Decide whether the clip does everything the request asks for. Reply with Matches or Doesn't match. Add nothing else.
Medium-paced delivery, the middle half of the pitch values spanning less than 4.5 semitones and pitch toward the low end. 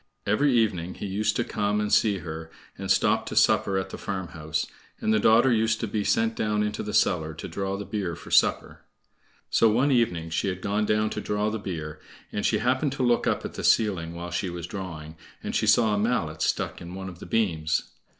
Doesn't match